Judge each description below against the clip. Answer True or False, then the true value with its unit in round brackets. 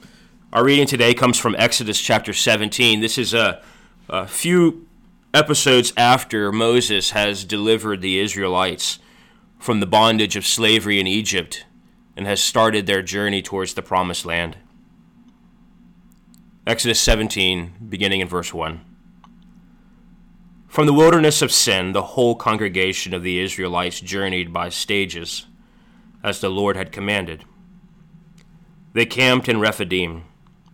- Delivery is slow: True (125 wpm)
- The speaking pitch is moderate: False (105 Hz)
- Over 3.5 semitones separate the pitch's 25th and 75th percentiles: True (4.7 semitones)